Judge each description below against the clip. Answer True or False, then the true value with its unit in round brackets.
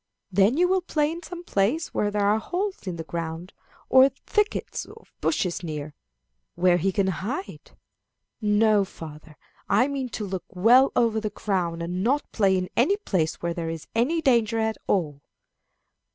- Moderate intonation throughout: False (7.0 semitones)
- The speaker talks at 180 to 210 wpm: False (170 wpm)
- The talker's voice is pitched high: True (210 Hz)